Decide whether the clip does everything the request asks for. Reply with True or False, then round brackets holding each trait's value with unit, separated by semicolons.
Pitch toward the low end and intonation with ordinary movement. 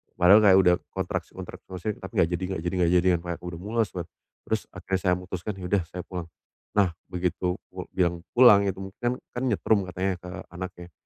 False (90 Hz; 1.8 semitones)